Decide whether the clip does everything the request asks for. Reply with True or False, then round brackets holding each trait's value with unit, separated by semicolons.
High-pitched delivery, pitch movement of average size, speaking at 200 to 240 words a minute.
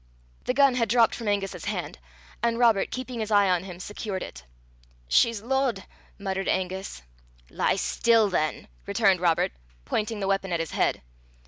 False (200 Hz; 3.6 semitones; 160 wpm)